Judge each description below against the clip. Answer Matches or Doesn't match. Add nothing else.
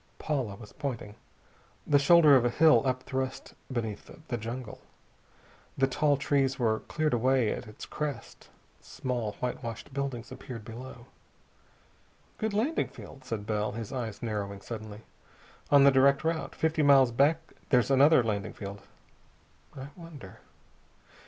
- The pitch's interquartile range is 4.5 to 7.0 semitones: Doesn't match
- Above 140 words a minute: Doesn't match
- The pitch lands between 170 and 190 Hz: Doesn't match